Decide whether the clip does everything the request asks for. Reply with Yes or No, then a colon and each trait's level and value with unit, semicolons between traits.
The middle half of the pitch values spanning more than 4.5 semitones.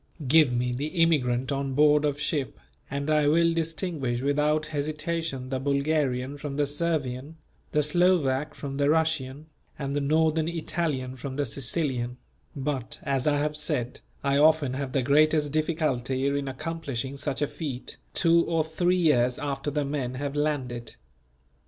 No: average, 2.8 semitones